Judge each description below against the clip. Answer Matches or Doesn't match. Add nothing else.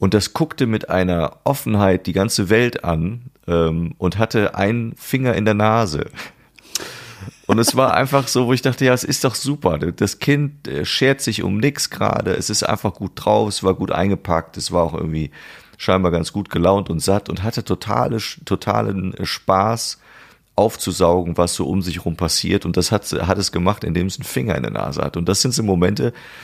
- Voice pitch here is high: Doesn't match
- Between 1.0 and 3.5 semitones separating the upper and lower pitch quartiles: Doesn't match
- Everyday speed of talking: Doesn't match